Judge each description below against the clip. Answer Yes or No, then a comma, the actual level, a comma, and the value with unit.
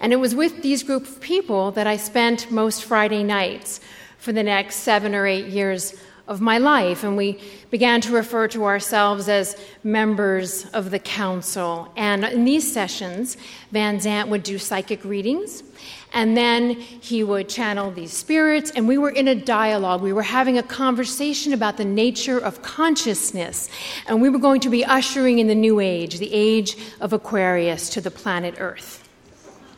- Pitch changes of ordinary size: Yes, average, 3.4 semitones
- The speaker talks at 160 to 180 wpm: Yes, average, 175 wpm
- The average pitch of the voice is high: Yes, high, 215 Hz